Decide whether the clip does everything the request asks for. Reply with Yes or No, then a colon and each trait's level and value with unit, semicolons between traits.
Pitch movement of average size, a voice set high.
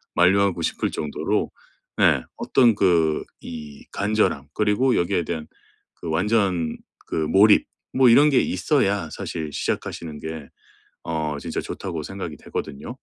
No: average, 4.8 semitones; very low, 85 Hz